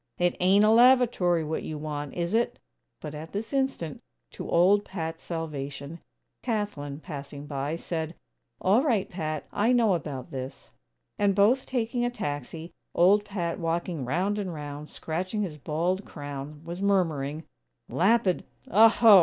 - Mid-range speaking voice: Yes, medium, 170 Hz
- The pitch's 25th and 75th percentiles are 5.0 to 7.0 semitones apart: Yes, average, 5.3 semitones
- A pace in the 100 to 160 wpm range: Yes, average, 145 wpm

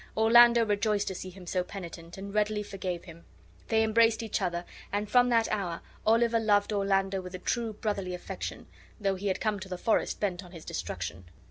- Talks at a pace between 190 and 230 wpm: Yes, average, 200 wpm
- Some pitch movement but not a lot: Yes, average, 3.2 semitones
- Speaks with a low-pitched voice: No, high, 200 Hz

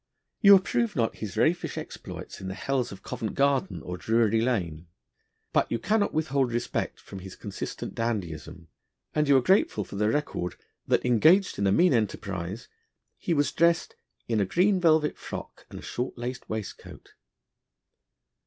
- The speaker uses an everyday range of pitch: No, wide, 7.8 semitones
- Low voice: Yes, low, 120 Hz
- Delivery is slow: No, average, 165 wpm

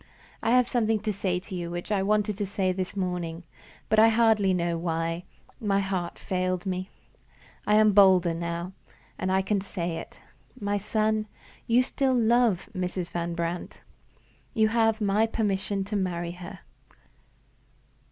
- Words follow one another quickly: No, average, 155 wpm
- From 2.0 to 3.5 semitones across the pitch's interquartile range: Yes, average, 3.2 semitones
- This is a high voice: Yes, high, 195 Hz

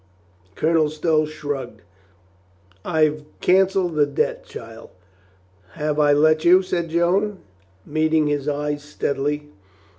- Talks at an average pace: No, slow, 110 wpm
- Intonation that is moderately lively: No, narrow, 2.1 semitones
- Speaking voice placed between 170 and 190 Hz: No, medium, 155 Hz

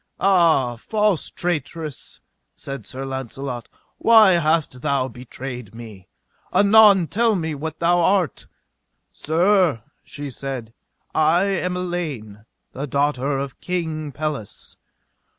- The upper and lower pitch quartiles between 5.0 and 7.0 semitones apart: Yes, average, 5.3 semitones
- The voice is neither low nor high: Yes, medium, 150 Hz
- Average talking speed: No, slow, 110 wpm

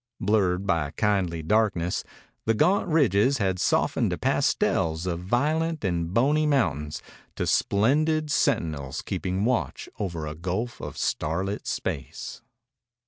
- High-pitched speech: No, low, 100 Hz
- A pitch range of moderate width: No, wide, 7.1 semitones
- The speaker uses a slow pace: Yes, slow, 125 wpm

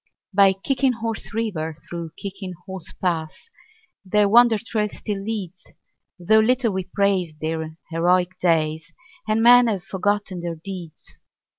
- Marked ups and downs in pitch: No, average, 4.1 semitones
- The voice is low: No, high, 190 Hz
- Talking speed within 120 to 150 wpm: Yes, slow, 135 wpm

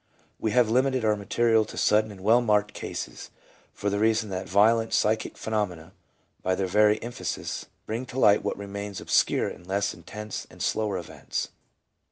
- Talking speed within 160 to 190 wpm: Yes, average, 170 wpm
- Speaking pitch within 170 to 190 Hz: No, low, 105 Hz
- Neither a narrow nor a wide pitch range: No, narrow, 1.9 semitones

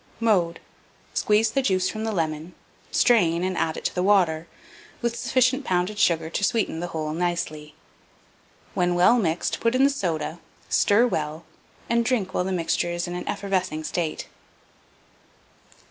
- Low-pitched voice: No, medium, 180 Hz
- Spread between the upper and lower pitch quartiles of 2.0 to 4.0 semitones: No, average, 4.7 semitones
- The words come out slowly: No, average, 160 wpm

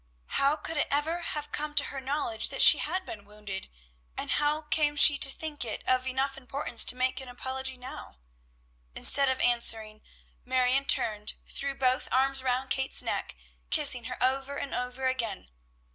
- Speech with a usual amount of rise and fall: No, narrow, 2.2 semitones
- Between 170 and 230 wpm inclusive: Yes, average, 175 wpm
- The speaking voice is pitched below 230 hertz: No, very high, 265 Hz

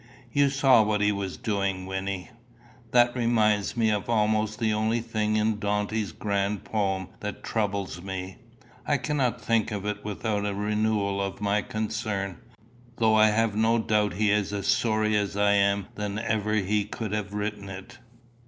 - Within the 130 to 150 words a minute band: No, average, 170 wpm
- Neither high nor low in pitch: No, low, 105 Hz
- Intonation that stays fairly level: Yes, narrow, 1.6 semitones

